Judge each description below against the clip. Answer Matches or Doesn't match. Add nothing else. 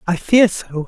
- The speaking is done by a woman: Doesn't match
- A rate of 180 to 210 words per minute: Matches